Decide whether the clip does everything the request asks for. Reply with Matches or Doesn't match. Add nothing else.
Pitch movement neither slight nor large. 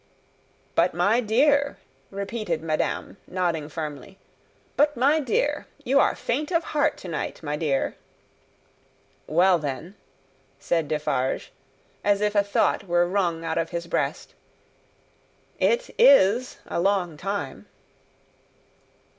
Doesn't match